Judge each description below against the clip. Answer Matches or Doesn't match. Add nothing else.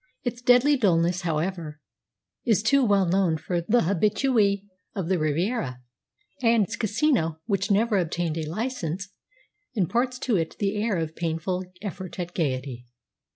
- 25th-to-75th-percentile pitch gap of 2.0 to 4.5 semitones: Doesn't match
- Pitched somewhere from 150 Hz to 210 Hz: Matches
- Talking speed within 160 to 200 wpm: Doesn't match